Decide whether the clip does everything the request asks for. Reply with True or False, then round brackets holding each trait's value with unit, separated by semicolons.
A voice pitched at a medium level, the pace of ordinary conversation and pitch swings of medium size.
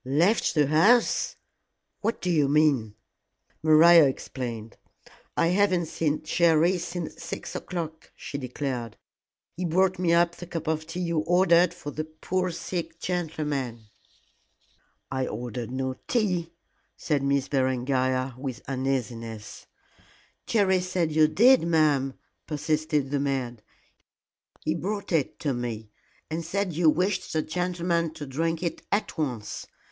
False (155 Hz; 130 wpm; 4.5 semitones)